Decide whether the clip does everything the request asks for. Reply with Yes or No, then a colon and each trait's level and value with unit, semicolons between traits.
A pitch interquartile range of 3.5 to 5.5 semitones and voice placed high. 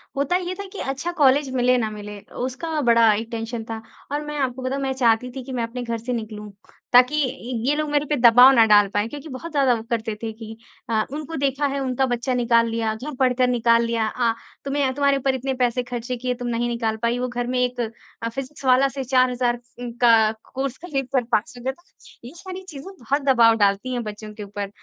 No: average, 2.9 semitones; very high, 250 Hz